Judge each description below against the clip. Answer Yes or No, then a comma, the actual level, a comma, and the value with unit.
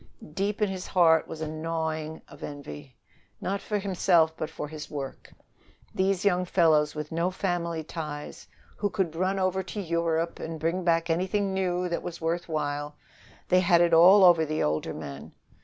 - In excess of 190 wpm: No, average, 175 wpm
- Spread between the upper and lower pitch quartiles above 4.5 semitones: No, average, 2.8 semitones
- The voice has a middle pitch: Yes, medium, 170 Hz